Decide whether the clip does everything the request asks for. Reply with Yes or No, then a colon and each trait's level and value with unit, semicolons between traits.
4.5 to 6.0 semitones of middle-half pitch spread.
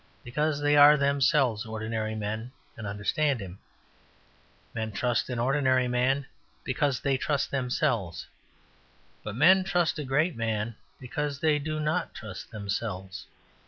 Yes: average, 5.0 semitones